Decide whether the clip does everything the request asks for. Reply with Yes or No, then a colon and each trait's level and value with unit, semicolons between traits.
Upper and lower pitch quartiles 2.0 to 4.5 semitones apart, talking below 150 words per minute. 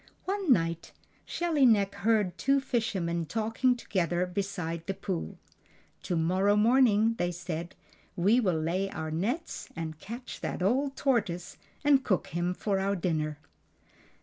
No: wide, 5.4 semitones; average, 140 wpm